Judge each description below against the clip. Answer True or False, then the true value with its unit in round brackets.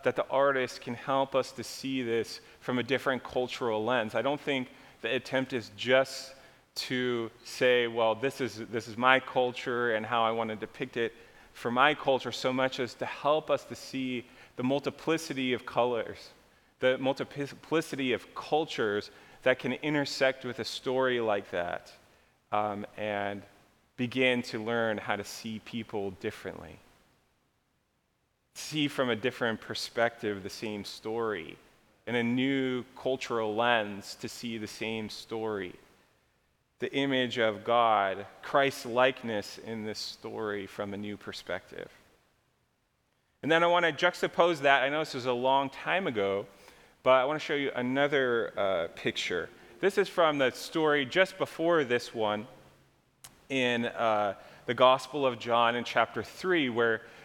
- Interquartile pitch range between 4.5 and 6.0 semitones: False (3.3 semitones)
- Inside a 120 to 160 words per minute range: True (155 wpm)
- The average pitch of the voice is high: False (125 Hz)